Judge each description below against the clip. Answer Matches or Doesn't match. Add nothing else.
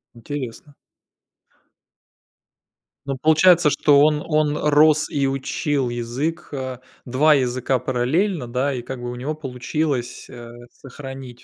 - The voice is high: Doesn't match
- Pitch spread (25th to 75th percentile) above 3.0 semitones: Matches